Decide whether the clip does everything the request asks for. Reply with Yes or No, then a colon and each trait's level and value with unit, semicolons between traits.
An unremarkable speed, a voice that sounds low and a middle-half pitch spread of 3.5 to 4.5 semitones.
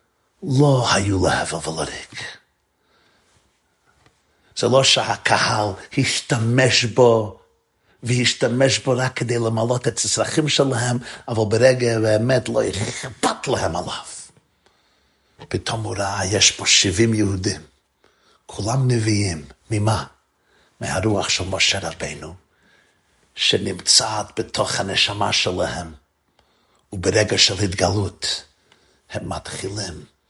No: slow, 95 wpm; low, 110 Hz; average, 4.2 semitones